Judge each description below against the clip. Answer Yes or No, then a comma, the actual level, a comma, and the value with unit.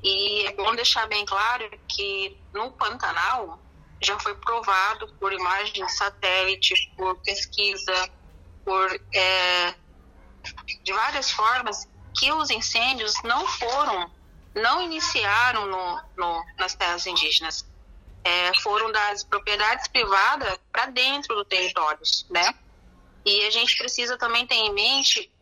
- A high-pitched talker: Yes, high, 205 Hz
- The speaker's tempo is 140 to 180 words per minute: No, average, 125 wpm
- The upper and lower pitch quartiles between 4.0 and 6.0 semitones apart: Yes, average, 4.4 semitones